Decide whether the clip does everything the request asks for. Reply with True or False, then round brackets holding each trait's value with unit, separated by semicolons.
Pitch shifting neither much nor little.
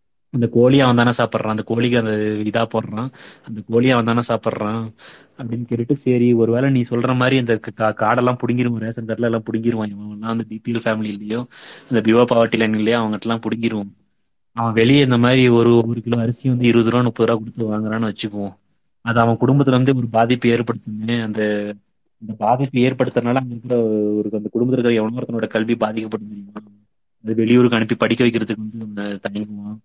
False (1.7 semitones)